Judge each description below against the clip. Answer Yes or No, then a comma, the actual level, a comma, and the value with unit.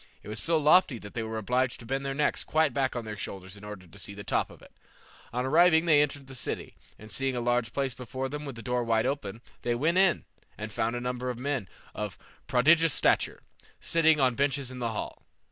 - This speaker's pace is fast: Yes, fast, 240 wpm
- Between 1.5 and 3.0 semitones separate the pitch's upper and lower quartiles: No, average, 4.1 semitones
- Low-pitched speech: Yes, low, 125 Hz